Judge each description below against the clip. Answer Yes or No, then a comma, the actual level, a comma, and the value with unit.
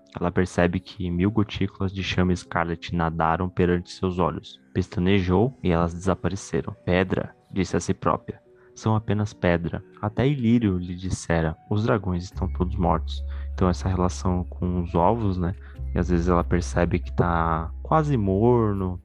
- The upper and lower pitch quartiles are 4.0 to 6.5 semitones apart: No, narrow, 2.4 semitones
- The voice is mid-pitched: No, very low, 90 Hz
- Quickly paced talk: No, average, 155 wpm